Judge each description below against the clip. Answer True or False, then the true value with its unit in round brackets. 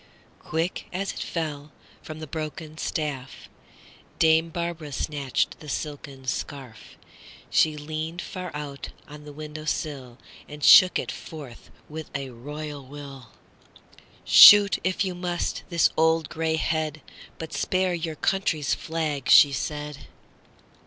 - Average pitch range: False (2.1 semitones)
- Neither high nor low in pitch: True (155 Hz)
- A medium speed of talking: False (115 wpm)